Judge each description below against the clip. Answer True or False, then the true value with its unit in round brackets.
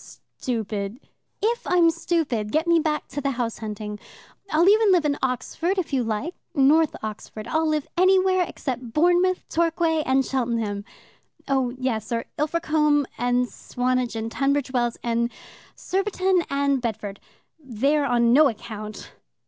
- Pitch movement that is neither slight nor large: False (5.7 semitones)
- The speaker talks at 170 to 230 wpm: False (145 wpm)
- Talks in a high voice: True (275 Hz)